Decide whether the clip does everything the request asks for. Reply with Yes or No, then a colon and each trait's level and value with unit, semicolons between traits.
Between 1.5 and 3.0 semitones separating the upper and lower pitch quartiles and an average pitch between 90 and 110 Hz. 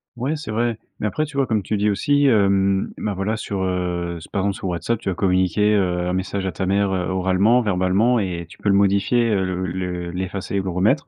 Yes: average, 2.7 semitones; very low, 95 Hz